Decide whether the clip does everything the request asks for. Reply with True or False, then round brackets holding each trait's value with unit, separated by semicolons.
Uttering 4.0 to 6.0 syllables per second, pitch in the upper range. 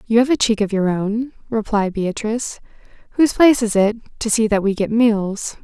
True (5.1 syllables/s; 220 Hz)